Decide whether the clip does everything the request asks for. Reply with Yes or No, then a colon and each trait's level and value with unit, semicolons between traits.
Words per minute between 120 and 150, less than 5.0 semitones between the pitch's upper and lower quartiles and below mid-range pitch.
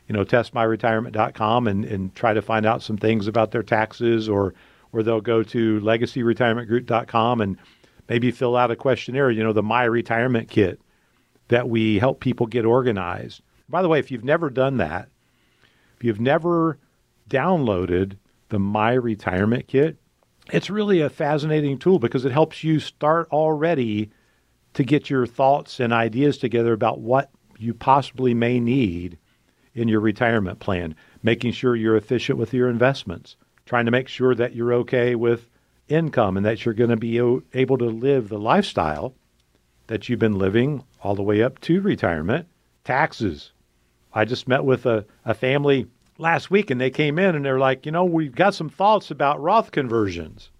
No: average, 170 wpm; average, 3.4 semitones; low, 120 Hz